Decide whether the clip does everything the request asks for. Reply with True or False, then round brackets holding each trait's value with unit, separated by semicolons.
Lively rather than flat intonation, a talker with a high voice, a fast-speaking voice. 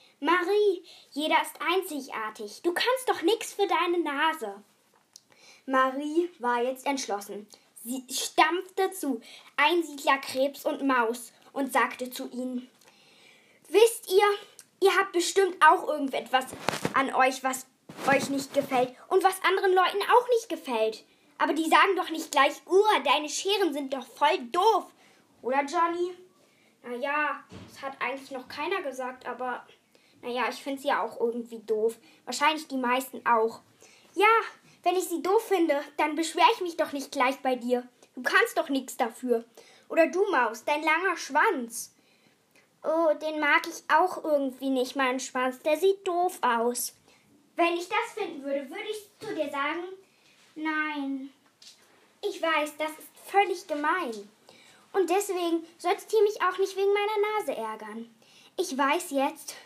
False (5.7 semitones; 300 Hz; 150 wpm)